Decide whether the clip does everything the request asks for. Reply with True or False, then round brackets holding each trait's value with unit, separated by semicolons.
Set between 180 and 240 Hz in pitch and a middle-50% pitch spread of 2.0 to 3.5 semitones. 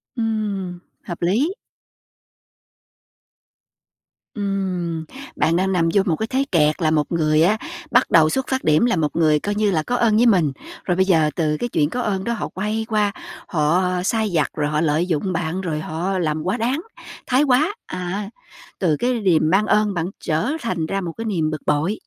False (185 Hz; 5.2 semitones)